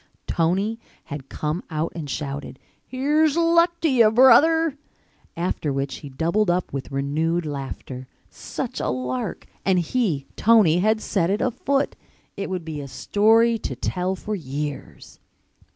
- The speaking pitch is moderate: Yes, medium, 180 Hz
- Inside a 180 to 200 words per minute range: No, average, 145 wpm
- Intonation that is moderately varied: No, wide, 7.8 semitones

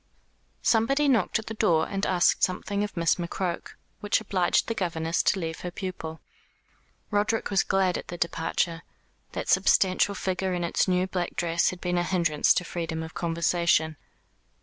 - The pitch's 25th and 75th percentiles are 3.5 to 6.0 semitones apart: No, narrow, 2.5 semitones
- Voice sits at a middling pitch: Yes, medium, 180 Hz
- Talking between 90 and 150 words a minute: No, average, 170 wpm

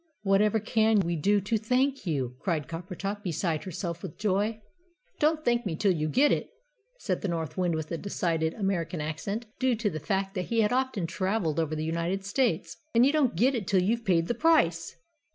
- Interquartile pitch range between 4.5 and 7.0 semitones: Yes, average, 5.2 semitones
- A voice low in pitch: No, high, 195 Hz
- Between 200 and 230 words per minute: Yes, fast, 205 wpm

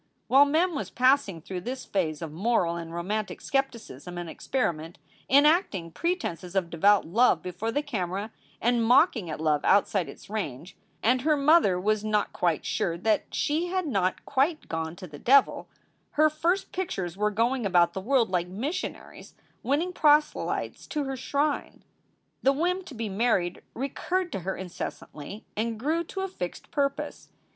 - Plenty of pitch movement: Yes, wide, 8.0 semitones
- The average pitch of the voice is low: No, high, 220 Hz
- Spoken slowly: No, average, 165 wpm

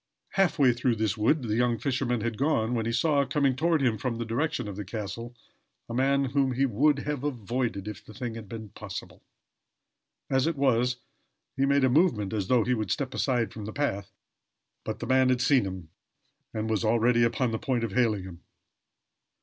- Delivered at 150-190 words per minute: No, fast, 205 wpm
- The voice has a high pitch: No, low, 120 Hz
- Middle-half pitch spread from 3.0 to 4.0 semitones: Yes, average, 3.6 semitones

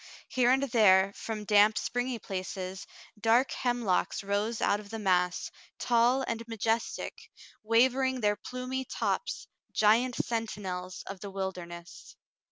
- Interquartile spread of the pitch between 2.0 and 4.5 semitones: Yes, average, 3.9 semitones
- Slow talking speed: Yes, slow, 125 wpm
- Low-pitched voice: No, high, 220 Hz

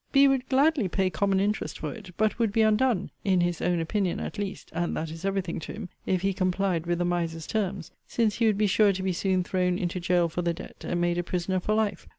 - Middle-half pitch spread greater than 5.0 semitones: No, average, 3.2 semitones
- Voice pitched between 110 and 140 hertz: No, high, 190 Hz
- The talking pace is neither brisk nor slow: No, fast, 255 wpm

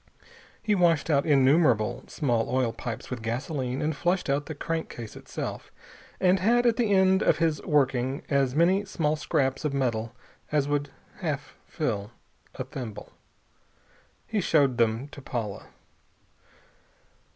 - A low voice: No, medium, 145 Hz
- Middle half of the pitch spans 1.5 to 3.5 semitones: No, average, 4.7 semitones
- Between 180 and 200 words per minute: No, average, 140 wpm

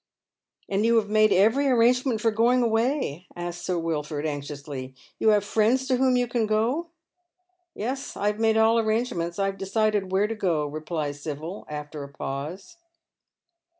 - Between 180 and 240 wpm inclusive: Yes, average, 185 wpm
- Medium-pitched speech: No, high, 210 Hz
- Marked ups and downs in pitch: Yes, wide, 6.3 semitones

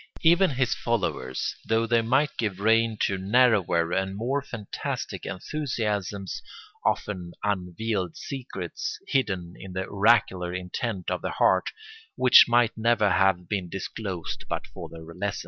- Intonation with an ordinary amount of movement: Yes, average, 4.3 semitones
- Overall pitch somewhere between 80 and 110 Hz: Yes, low, 105 Hz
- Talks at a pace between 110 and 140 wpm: Yes, slow, 135 wpm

